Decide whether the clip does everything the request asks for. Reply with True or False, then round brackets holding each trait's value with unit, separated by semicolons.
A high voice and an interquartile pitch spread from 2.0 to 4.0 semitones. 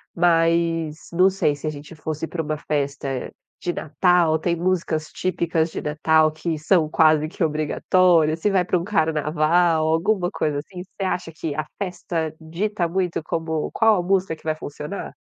False (165 Hz; 2.4 semitones)